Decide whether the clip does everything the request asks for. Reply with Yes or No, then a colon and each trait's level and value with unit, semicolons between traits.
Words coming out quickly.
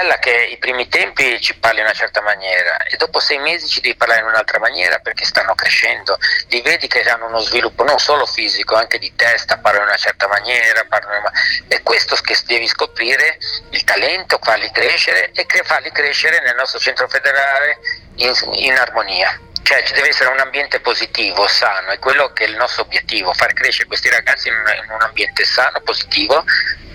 Yes: fast, 185 wpm